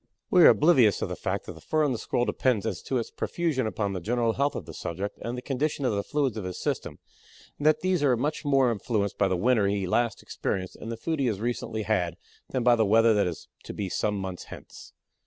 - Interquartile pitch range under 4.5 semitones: No, average, 4.9 semitones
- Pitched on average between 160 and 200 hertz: No, low, 115 Hz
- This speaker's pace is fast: Yes, fast, 250 wpm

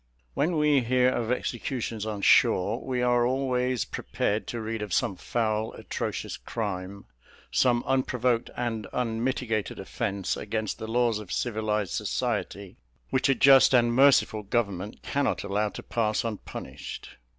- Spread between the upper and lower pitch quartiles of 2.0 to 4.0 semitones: Yes, average, 3.0 semitones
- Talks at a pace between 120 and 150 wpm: Yes, average, 140 wpm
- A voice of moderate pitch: No, low, 115 Hz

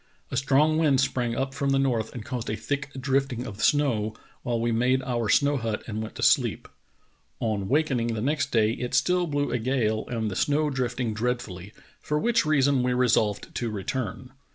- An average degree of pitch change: Yes, average, 3.6 semitones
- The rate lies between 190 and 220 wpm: Yes, average, 195 wpm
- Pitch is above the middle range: No, low, 125 Hz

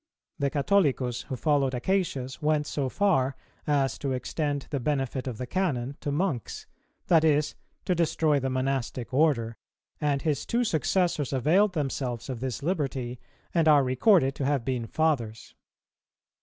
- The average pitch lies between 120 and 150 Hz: Yes, medium, 140 Hz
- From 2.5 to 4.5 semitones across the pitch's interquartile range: Yes, average, 3.4 semitones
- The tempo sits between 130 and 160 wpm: Yes, average, 150 wpm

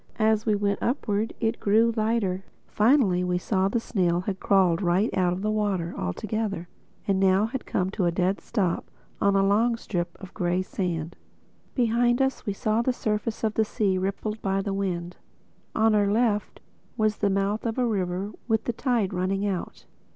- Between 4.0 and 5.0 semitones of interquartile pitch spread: No, average, 2.9 semitones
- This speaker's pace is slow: No, average, 190 wpm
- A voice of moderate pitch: No, high, 200 Hz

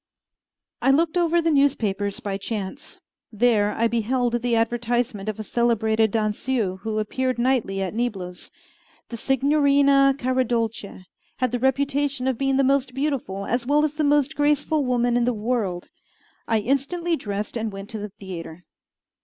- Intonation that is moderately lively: Yes, average, 4.4 semitones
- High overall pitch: Yes, high, 240 Hz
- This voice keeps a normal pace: Yes, average, 155 wpm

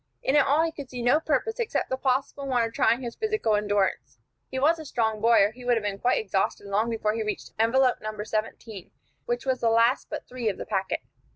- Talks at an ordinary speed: No, fast, 240 wpm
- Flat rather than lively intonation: No, average, 3.6 semitones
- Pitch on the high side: Yes, high, 235 Hz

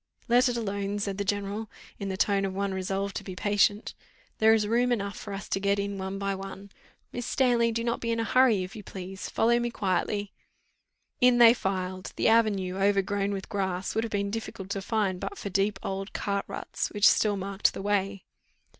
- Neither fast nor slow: No, fast, 210 wpm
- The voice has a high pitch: Yes, high, 200 Hz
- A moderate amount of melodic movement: No, narrow, 2.3 semitones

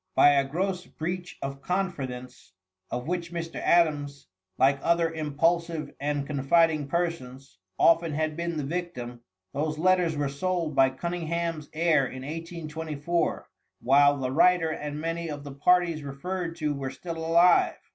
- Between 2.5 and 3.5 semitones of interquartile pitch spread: Yes, average, 3.2 semitones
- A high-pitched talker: No, medium, 155 Hz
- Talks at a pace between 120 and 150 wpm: Yes, average, 145 wpm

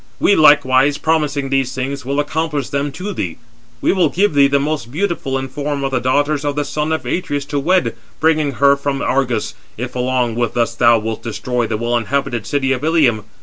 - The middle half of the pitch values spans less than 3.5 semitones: Yes, average, 2.8 semitones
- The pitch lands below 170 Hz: Yes, medium, 140 Hz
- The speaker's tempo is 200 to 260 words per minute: Yes, fast, 205 wpm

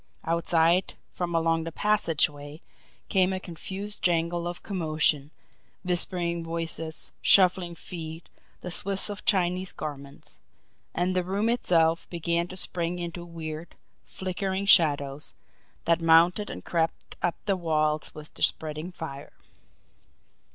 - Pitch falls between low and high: Yes, medium, 170 Hz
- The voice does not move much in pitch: Yes, narrow, 2.2 semitones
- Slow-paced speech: Yes, slow, 125 wpm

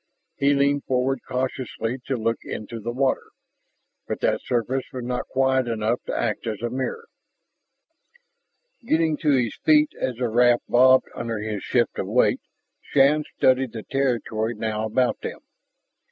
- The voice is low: Yes, low, 125 Hz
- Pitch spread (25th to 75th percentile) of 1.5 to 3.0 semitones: Yes, average, 2.7 semitones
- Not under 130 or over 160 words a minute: Yes, average, 155 wpm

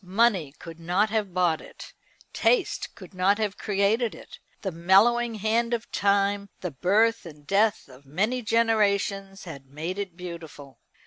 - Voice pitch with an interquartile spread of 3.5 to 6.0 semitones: Yes, average, 4.3 semitones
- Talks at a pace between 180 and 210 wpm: No, average, 150 wpm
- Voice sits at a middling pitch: No, high, 195 Hz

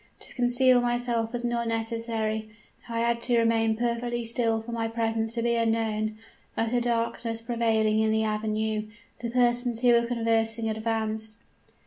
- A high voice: Yes, high, 230 Hz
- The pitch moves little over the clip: Yes, narrow, 1.2 semitones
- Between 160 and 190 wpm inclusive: No, average, 150 wpm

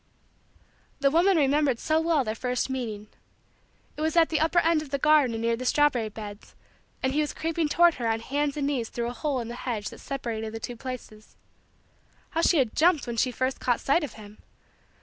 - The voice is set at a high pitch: Yes, very high, 265 Hz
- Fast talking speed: Yes, fast, 210 wpm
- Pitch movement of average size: Yes, average, 4.7 semitones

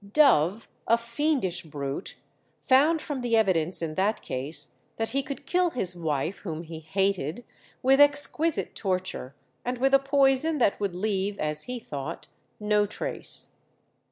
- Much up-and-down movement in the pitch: Yes, wide, 8.2 semitones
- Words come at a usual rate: Yes, average, 150 wpm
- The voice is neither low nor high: No, high, 205 Hz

